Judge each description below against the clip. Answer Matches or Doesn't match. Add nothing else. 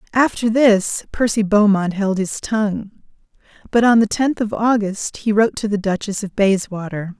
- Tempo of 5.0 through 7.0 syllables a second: Doesn't match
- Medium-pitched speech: Doesn't match